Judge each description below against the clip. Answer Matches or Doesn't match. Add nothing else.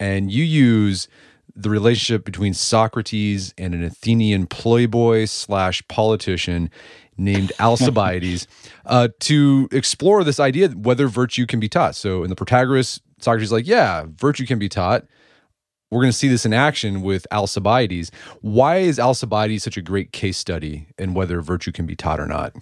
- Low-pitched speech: Matches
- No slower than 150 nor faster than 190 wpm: Matches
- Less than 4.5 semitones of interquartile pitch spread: Doesn't match